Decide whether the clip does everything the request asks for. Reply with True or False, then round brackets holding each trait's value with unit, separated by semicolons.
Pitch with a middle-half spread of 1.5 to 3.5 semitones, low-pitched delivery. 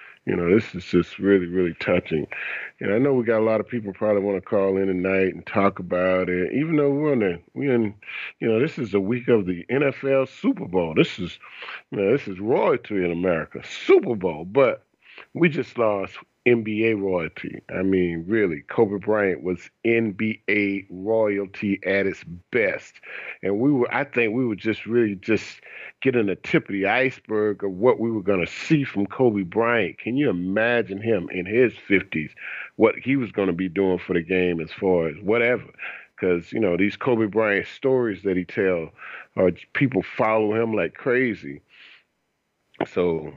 False (4.0 semitones; 105 Hz)